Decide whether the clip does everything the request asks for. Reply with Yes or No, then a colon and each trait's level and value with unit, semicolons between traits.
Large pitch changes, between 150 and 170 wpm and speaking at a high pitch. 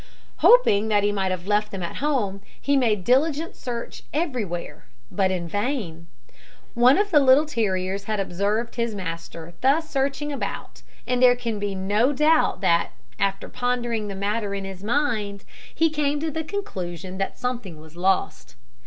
Yes: wide, 6.0 semitones; average, 165 wpm; high, 215 Hz